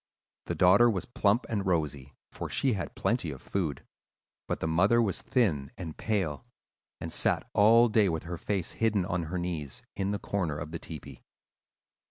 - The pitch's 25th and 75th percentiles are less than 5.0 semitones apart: Yes, average, 4.4 semitones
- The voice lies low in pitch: Yes, very low, 90 Hz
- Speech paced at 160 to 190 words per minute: Yes, average, 180 wpm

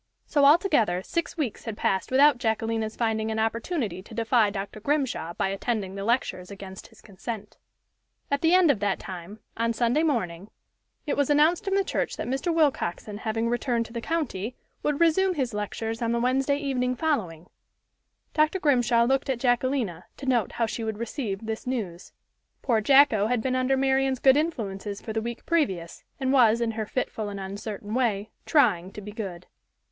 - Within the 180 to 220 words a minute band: Yes, average, 185 wpm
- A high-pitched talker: Yes, high, 230 Hz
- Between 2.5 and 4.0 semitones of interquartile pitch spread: No, average, 4.5 semitones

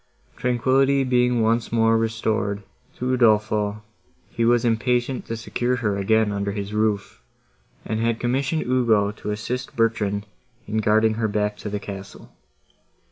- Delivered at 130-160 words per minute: Yes, average, 140 wpm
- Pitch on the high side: No, low, 110 Hz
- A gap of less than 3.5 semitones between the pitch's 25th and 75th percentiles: Yes, narrow, 2.6 semitones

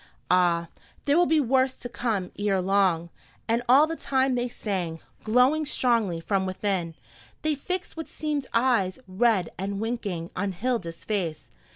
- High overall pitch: Yes, high, 210 Hz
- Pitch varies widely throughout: Yes, wide, 6.0 semitones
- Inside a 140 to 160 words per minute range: Yes, average, 155 wpm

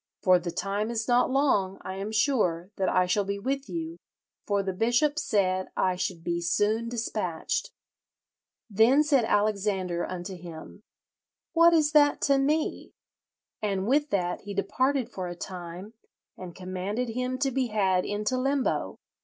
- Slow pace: No, average, 155 wpm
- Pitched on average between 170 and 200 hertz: No, high, 210 Hz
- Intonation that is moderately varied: No, wide, 5.8 semitones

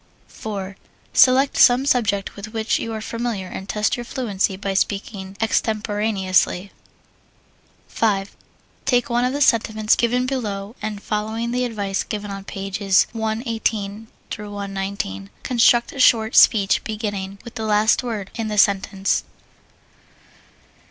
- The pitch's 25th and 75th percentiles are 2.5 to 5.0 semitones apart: Yes, average, 2.8 semitones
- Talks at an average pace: No, slow, 130 wpm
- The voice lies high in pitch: Yes, high, 215 Hz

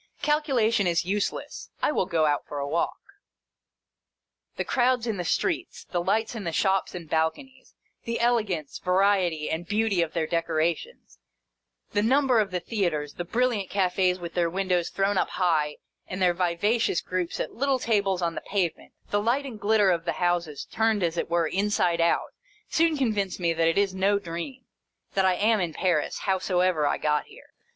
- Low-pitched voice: No, medium, 185 Hz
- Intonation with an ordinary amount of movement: Yes, average, 4.3 semitones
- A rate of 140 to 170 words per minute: No, average, 185 wpm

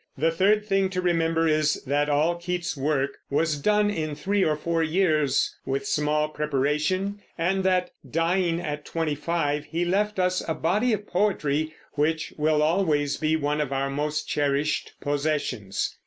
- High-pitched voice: No, medium, 155 Hz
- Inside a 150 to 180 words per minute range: Yes, average, 160 wpm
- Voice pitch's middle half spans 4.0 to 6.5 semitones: No, average, 3.3 semitones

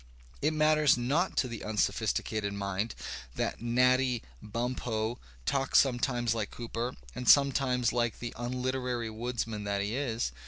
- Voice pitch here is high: No, low, 120 Hz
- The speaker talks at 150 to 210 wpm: No, slow, 135 wpm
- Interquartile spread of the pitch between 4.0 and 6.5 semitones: No, narrow, 2.5 semitones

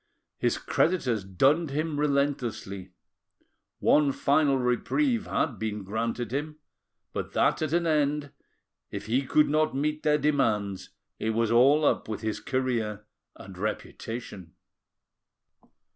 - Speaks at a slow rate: Yes, slow, 125 wpm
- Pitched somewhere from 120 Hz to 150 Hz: Yes, low, 135 Hz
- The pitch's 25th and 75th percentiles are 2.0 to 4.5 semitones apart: No, wide, 5.4 semitones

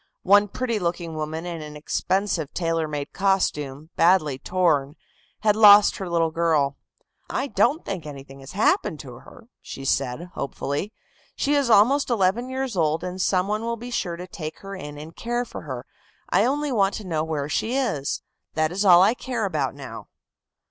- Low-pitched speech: No, medium, 180 Hz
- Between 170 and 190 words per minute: Yes, average, 185 wpm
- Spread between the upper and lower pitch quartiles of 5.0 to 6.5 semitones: Yes, wide, 5.6 semitones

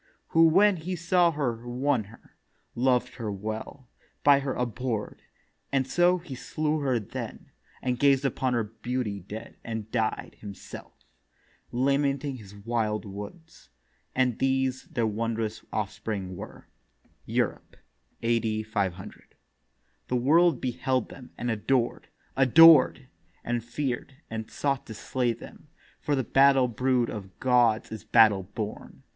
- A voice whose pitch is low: Yes, low, 125 Hz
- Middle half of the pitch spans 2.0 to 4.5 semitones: Yes, average, 3.9 semitones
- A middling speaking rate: No, slow, 130 wpm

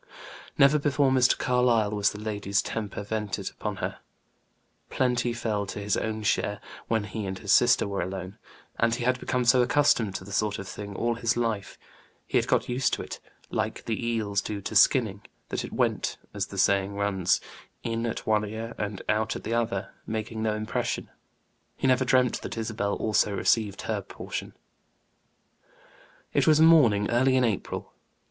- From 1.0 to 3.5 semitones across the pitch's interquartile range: Yes, average, 2.9 semitones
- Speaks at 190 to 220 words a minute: No, average, 180 wpm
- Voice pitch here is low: Yes, low, 110 Hz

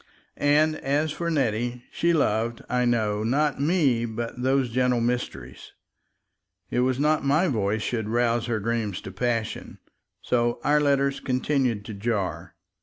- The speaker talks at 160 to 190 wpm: No, average, 145 wpm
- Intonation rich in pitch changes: No, average, 3.7 semitones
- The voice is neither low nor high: No, low, 120 Hz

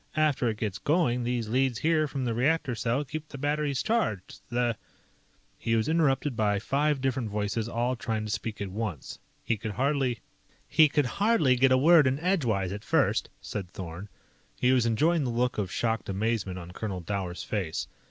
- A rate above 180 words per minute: Yes, average, 190 wpm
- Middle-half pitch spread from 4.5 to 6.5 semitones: Yes, average, 5.1 semitones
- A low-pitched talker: Yes, low, 120 Hz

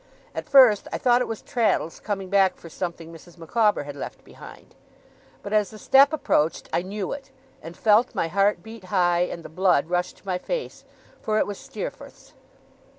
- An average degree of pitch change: Yes, average, 4.2 semitones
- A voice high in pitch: Yes, high, 195 Hz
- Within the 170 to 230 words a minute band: Yes, average, 190 wpm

